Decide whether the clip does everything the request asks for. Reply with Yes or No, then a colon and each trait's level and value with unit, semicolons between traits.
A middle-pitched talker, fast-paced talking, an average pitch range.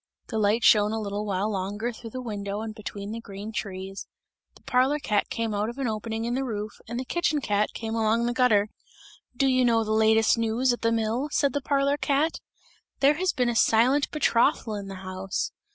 No: high, 225 Hz; fast, 215 wpm; average, 3.2 semitones